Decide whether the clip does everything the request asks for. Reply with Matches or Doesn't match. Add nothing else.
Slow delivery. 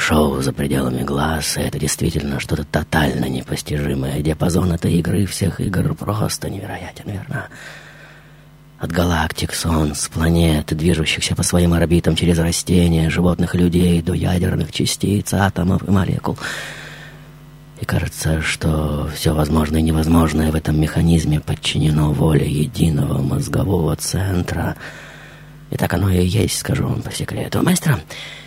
Doesn't match